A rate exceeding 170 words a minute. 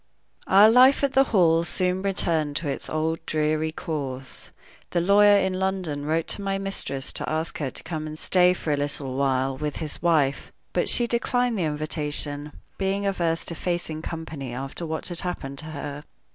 Yes: average, 185 wpm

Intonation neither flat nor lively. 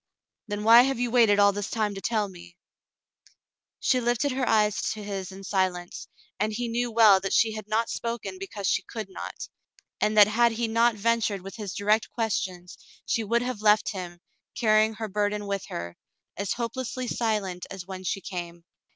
Yes: average, 3.0 semitones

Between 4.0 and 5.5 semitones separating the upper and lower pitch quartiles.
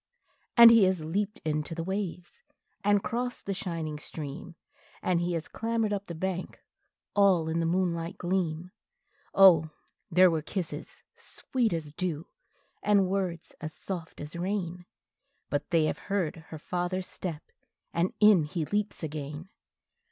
No: average, 3.3 semitones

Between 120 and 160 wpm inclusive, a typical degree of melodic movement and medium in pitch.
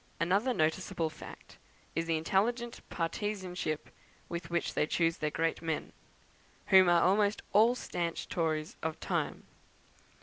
Yes: slow, 135 wpm; average, 3.5 semitones; medium, 170 Hz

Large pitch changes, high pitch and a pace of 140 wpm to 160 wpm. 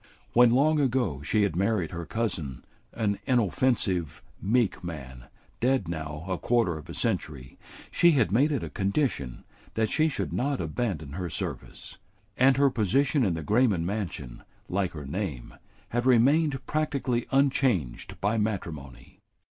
No: wide, 7.7 semitones; low, 105 Hz; average, 145 wpm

